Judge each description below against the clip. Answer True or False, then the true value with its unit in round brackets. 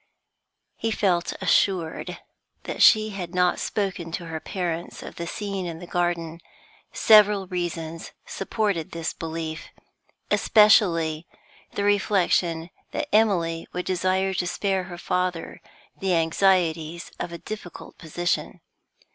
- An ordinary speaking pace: False (120 wpm)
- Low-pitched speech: False (175 Hz)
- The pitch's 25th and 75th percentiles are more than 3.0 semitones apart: False (2.7 semitones)